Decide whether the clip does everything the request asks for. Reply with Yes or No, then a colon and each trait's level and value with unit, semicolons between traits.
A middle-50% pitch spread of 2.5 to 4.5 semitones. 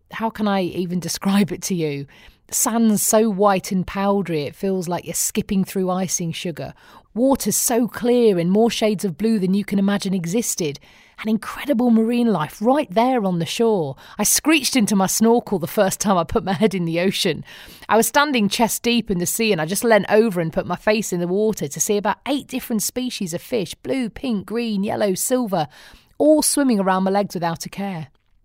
Yes: average, 3.8 semitones